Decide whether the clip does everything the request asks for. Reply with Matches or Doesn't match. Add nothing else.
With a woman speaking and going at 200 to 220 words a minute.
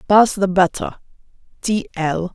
Doesn't match